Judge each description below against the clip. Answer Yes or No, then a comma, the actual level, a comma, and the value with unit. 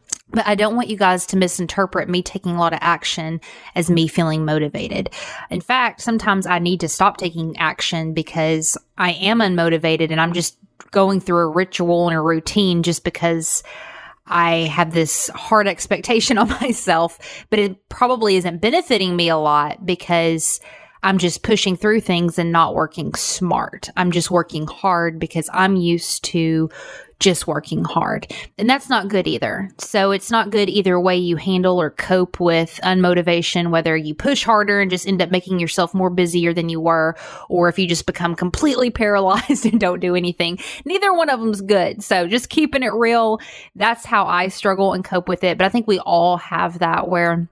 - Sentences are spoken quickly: No, average, 185 wpm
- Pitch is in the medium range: Yes, medium, 180 Hz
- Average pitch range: Yes, average, 3.1 semitones